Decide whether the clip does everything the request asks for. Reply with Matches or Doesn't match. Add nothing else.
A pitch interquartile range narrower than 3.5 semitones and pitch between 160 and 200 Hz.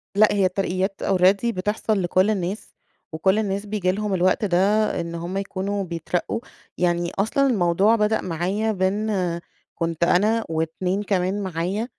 Matches